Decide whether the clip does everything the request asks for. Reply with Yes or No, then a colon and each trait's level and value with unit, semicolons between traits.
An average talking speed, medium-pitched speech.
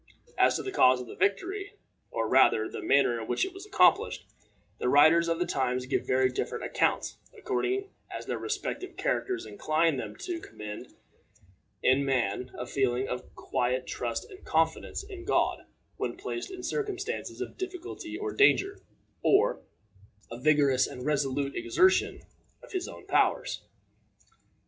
Yes: average, 155 wpm; medium, 170 Hz